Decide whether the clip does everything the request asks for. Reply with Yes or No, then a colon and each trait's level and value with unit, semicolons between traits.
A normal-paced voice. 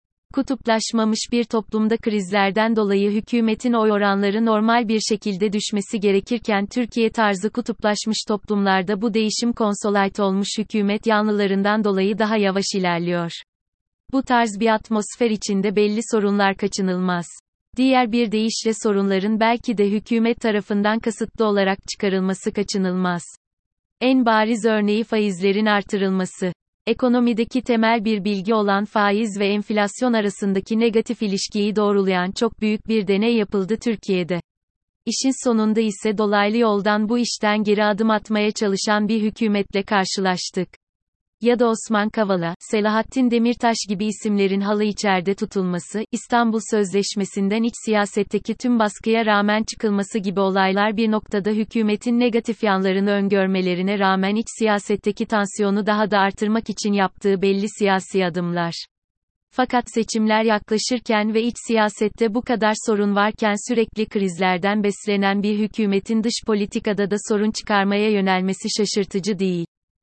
Yes: average, 125 wpm